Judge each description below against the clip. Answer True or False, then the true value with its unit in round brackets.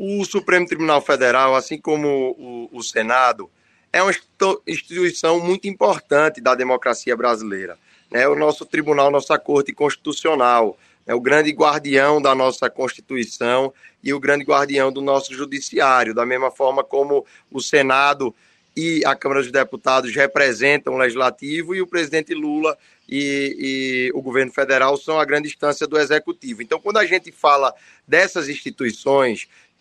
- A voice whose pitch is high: False (140 Hz)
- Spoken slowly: False (150 wpm)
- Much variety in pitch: False (2.7 semitones)